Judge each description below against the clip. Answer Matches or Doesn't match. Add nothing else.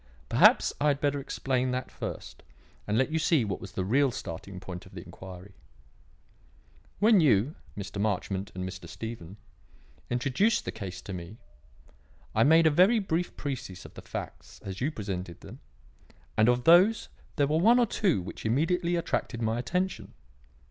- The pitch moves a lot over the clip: Matches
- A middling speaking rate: Matches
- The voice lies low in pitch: Matches